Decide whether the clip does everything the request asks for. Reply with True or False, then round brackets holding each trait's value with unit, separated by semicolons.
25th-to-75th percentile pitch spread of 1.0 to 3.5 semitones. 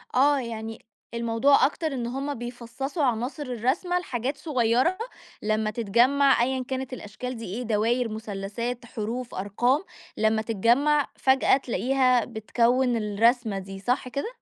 True (3.0 semitones)